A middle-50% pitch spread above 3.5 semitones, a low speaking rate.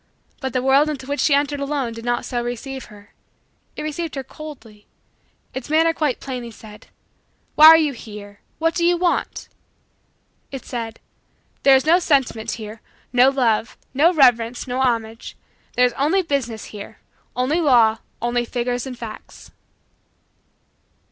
No: average, 3.9 semitones; average, 155 wpm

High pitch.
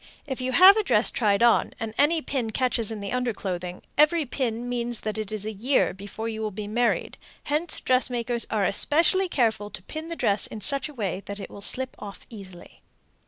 Yes: high, 230 Hz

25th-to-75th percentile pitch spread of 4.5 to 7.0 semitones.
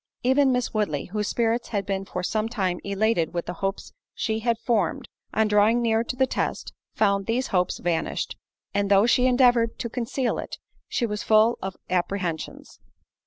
No: average, 3.4 semitones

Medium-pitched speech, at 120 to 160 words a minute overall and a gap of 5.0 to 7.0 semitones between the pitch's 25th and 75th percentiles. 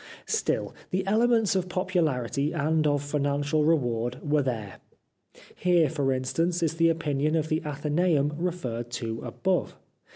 No: medium, 150 Hz; slow, 135 wpm; average, 3.7 semitones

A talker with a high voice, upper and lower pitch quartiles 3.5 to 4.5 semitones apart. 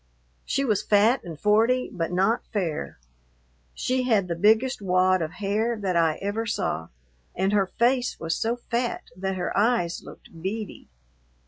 Yes: high, 205 Hz; average, 4.2 semitones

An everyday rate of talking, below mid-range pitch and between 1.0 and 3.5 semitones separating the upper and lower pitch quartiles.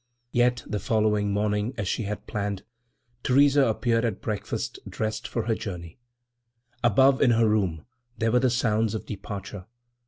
Yes: average, 155 wpm; low, 110 Hz; average, 2.7 semitones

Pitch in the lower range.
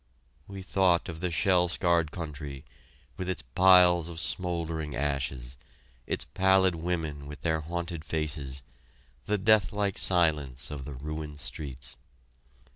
Yes: very low, 80 Hz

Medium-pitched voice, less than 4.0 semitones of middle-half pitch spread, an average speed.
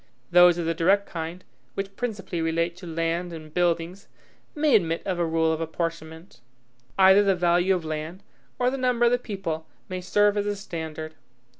Yes: medium, 175 Hz; average, 3.1 semitones; average, 180 wpm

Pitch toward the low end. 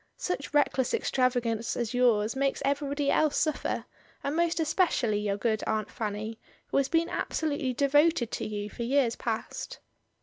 No: very high, 255 Hz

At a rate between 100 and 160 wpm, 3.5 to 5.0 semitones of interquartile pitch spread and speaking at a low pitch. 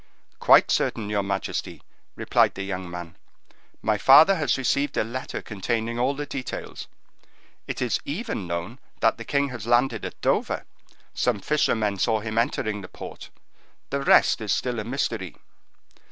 Yes: average, 155 wpm; average, 4.5 semitones; low, 115 Hz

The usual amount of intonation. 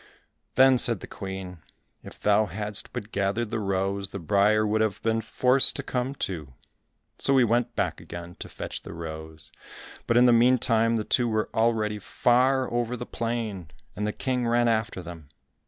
Yes: average, 3.6 semitones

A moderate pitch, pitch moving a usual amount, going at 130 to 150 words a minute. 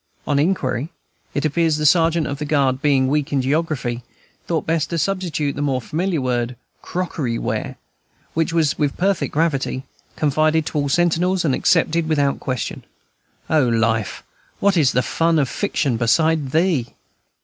No: medium, 150 Hz; average, 3.6 semitones; average, 165 wpm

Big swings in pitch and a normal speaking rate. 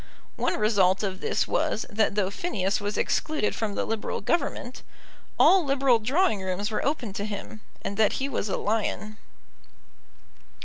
No: average, 3.9 semitones; average, 160 wpm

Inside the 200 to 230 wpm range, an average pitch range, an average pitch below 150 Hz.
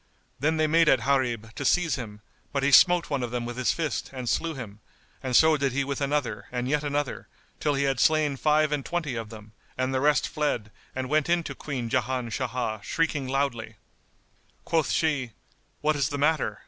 Yes: fast, 205 wpm; average, 3.6 semitones; low, 135 Hz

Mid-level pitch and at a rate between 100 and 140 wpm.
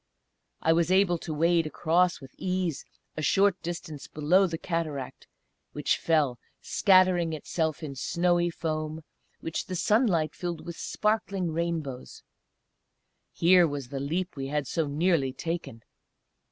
Yes: medium, 165 Hz; slow, 135 wpm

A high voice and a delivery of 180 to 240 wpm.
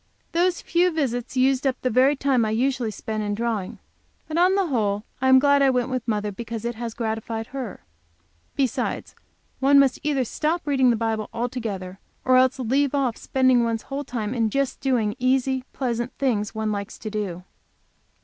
Yes: very high, 250 Hz; average, 185 wpm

